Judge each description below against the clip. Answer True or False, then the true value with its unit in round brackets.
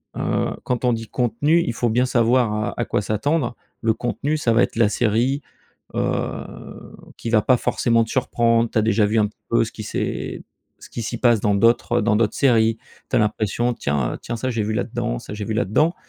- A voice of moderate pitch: False (115 Hz)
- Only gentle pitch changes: True (2.2 semitones)